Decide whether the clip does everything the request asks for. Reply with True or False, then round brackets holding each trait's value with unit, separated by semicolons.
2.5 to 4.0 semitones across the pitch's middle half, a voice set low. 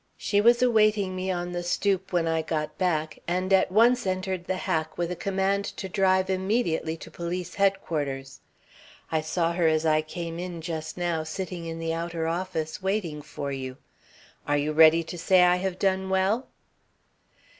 False (2.9 semitones; 175 Hz)